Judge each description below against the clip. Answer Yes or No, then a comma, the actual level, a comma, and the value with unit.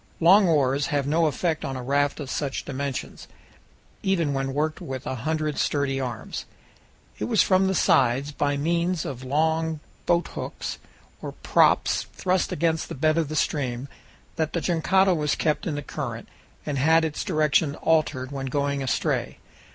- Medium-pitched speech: Yes, medium, 150 Hz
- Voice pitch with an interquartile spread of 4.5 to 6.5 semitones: No, average, 3.0 semitones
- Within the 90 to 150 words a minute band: No, average, 165 wpm